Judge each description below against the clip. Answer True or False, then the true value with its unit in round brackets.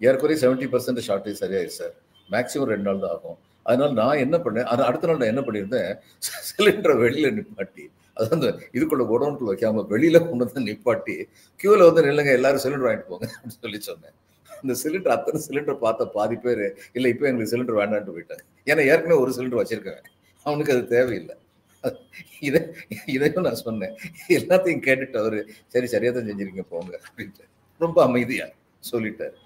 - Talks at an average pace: False (160 wpm)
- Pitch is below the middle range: True (125 Hz)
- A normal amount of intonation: False (7.4 semitones)